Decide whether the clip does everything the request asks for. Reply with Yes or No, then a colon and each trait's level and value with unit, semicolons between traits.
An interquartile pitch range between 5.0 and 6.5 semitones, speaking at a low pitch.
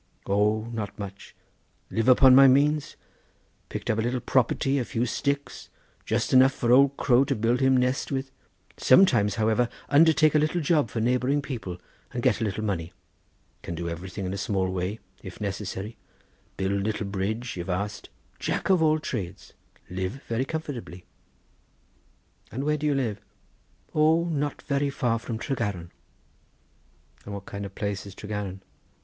Yes: wide, 5.4 semitones; low, 115 Hz